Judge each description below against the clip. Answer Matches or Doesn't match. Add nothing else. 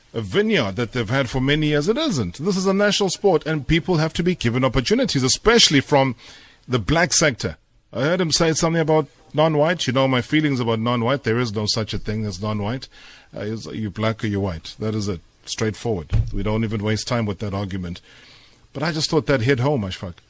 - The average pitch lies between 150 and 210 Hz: Doesn't match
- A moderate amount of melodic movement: Doesn't match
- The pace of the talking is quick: Matches